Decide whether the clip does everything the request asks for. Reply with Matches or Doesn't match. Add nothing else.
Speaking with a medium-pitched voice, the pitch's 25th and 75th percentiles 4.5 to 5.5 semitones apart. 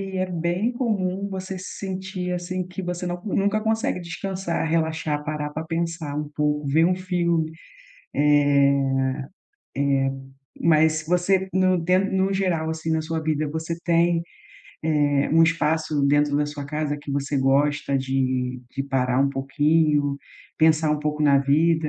Doesn't match